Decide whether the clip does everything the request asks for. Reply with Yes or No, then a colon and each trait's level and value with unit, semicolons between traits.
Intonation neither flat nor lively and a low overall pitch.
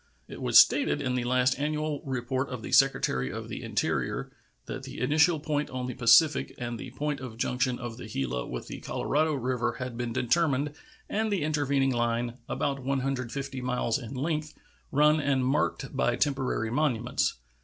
Yes: average, 3.2 semitones; low, 130 Hz